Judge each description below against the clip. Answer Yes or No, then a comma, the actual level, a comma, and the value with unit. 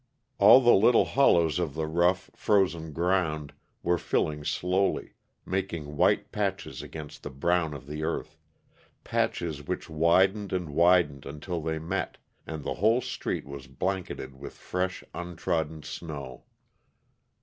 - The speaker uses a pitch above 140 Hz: No, very low, 85 Hz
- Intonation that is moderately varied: Yes, average, 3.4 semitones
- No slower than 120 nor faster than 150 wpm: Yes, slow, 135 wpm